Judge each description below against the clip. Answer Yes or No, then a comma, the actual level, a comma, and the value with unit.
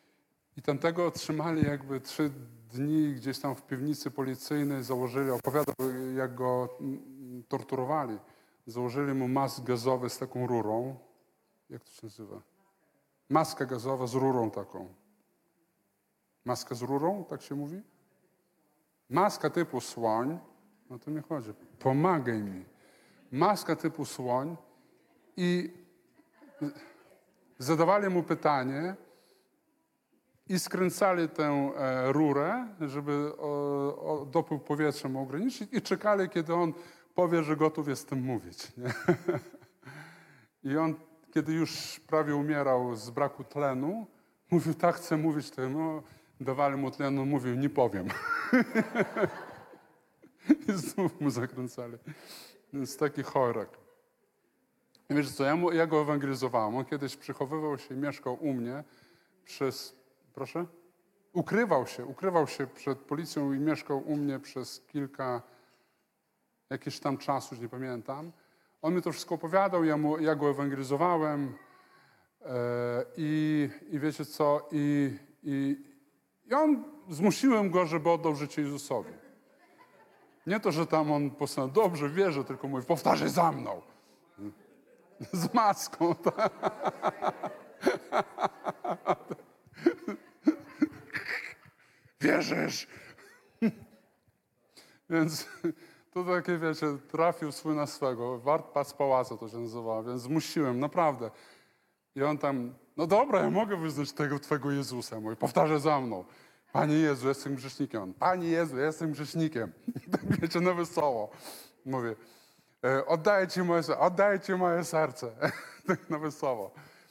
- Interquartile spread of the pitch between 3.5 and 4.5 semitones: Yes, average, 4.0 semitones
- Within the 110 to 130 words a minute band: Yes, average, 120 wpm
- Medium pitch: Yes, medium, 150 Hz